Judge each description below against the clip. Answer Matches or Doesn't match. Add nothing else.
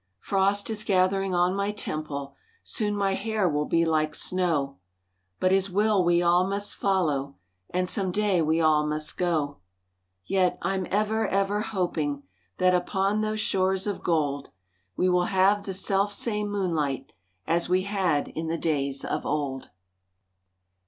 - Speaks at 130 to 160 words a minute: Matches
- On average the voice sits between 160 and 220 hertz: Matches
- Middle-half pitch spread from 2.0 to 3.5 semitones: Doesn't match